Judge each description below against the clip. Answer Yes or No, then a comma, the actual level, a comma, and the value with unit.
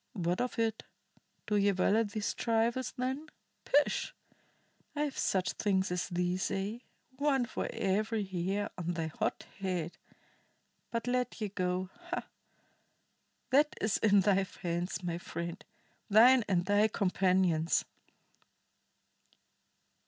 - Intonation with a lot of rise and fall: No, average, 4.1 semitones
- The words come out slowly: Yes, slow, 125 wpm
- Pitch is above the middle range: Yes, high, 200 Hz